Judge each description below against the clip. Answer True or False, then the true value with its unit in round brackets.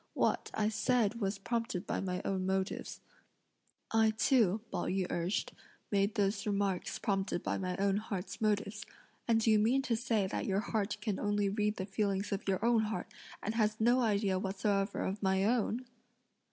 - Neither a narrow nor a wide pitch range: False (2.1 semitones)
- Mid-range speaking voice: False (205 Hz)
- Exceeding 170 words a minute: True (180 wpm)